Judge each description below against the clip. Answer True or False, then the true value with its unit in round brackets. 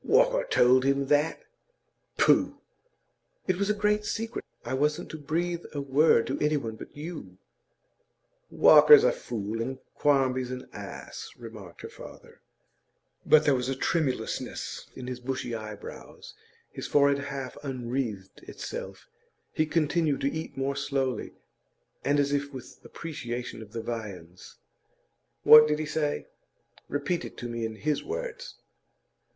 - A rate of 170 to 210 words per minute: False (145 wpm)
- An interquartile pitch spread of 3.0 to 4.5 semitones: True (4.1 semitones)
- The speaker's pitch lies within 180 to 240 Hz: False (140 Hz)